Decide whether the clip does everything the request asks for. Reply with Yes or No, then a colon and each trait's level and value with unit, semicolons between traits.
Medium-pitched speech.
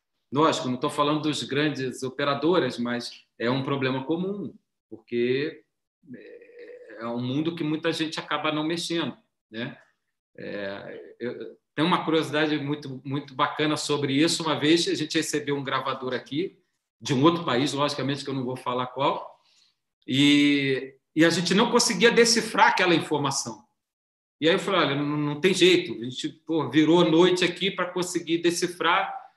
Yes: medium, 150 Hz